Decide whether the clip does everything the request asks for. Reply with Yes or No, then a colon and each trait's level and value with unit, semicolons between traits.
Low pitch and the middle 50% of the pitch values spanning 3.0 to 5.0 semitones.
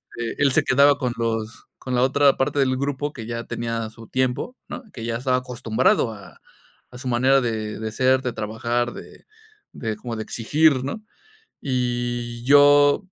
No: low, 125 Hz; narrow, 2.6 semitones